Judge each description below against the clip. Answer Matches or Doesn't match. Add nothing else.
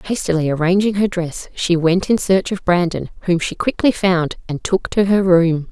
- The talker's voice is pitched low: Doesn't match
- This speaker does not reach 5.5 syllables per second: Matches